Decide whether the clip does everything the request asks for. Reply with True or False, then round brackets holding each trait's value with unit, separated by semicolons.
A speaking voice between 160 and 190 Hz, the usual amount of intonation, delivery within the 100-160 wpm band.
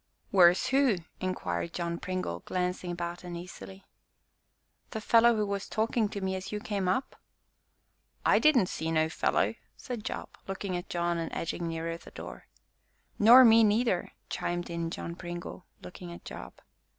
True (185 Hz; 3.5 semitones; 155 wpm)